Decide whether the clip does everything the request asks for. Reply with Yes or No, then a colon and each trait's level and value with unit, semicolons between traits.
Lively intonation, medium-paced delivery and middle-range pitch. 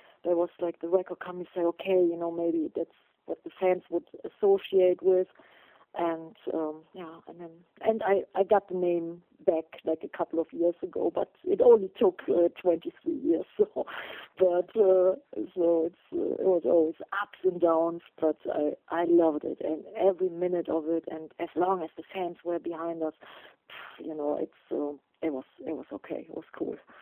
No: narrow, 2.6 semitones; average, 195 wpm; medium, 175 Hz